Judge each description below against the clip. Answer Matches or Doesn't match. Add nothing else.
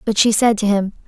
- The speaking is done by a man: Doesn't match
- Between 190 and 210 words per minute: Doesn't match